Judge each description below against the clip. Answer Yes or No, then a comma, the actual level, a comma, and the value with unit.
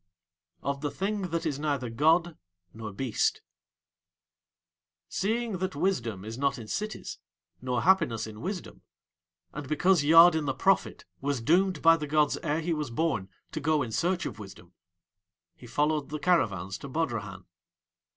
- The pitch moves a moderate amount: No, wide, 5.9 semitones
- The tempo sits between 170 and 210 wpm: No, average, 150 wpm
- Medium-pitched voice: Yes, medium, 150 Hz